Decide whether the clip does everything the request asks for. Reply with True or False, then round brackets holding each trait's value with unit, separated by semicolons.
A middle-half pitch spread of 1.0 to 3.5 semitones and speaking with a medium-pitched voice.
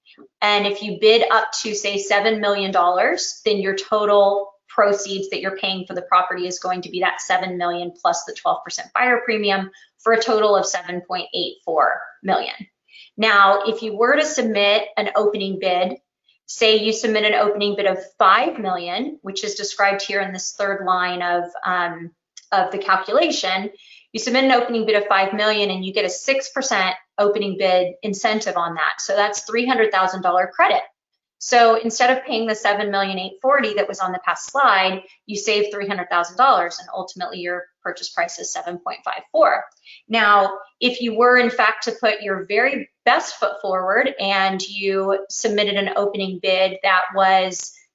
False (2.8 semitones; 200 Hz)